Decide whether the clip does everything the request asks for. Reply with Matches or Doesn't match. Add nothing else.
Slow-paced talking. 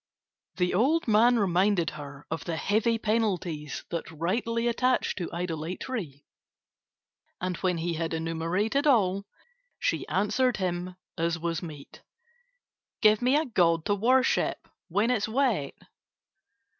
Matches